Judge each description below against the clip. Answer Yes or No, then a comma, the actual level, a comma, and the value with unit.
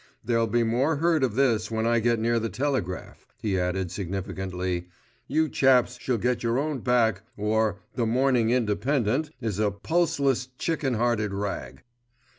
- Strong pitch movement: No, average, 4.1 semitones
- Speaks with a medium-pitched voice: No, low, 115 Hz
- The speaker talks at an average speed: Yes, average, 155 wpm